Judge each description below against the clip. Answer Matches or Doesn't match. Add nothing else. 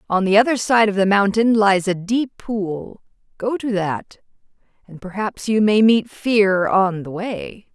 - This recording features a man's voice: Doesn't match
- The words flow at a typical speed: Matches